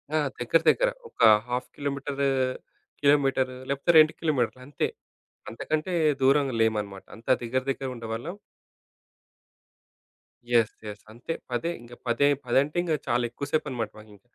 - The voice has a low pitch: Yes, low, 130 Hz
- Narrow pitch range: No, average, 3.5 semitones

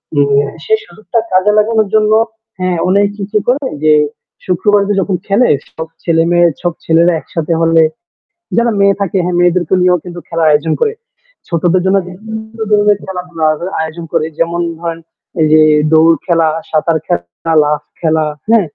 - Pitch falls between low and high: Yes, medium, 175 Hz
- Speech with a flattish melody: No, average, 3.8 semitones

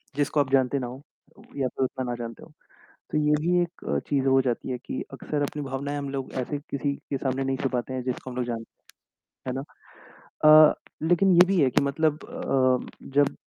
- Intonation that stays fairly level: Yes, narrow, 2.2 semitones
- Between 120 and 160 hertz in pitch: Yes, low, 135 Hz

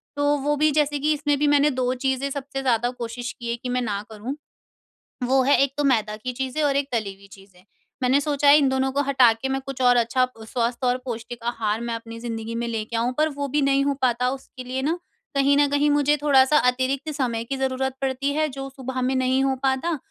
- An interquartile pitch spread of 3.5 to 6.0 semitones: No, average, 2.7 semitones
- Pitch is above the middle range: Yes, very high, 265 Hz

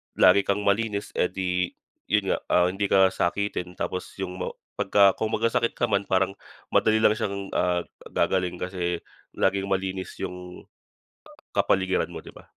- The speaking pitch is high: No, very low, 95 Hz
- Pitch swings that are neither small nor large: No, narrow, 1.9 semitones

